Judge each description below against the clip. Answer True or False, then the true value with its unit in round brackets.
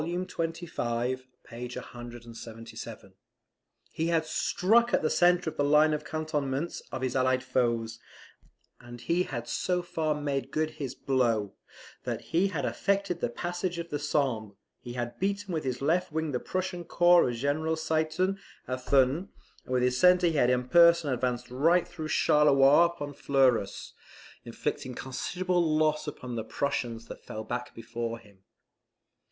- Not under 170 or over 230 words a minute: False (155 wpm)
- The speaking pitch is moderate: True (145 Hz)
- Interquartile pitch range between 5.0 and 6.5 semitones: True (5.4 semitones)